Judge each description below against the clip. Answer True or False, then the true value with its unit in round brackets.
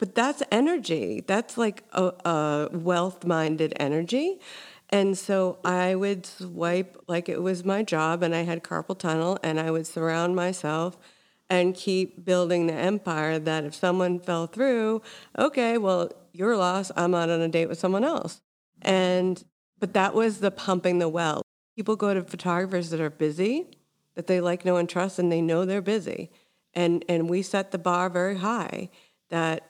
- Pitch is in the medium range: True (180 Hz)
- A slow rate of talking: False (175 wpm)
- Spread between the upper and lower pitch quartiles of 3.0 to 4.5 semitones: False (2.6 semitones)